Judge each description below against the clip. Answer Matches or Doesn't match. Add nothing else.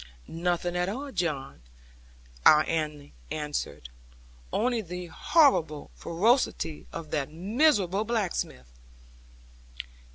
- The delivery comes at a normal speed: Doesn't match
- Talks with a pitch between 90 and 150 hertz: Doesn't match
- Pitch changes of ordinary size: Doesn't match